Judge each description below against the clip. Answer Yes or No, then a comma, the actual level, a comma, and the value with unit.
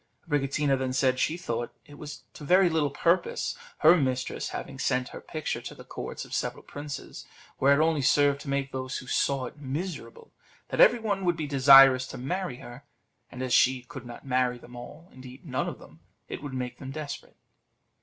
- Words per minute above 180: Yes, average, 200 wpm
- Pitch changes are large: No, average, 3.0 semitones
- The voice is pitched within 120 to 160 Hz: Yes, medium, 140 Hz